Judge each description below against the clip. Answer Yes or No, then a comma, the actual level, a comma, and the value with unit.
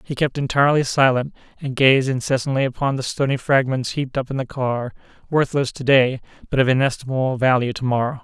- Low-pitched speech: Yes, low, 130 Hz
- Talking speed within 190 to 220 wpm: No, average, 175 wpm